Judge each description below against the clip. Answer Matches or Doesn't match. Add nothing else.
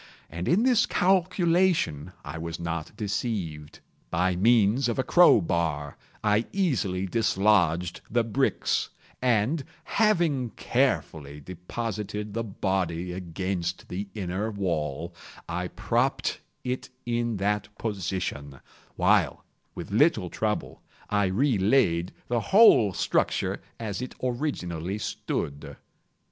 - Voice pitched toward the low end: Matches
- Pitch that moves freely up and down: Matches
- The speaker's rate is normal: Doesn't match